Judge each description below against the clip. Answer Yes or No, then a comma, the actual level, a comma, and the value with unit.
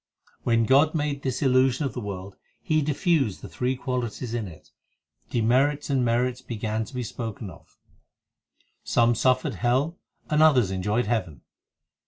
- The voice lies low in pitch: Yes, low, 125 Hz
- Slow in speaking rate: No, average, 155 wpm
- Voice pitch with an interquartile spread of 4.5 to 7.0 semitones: No, average, 3.5 semitones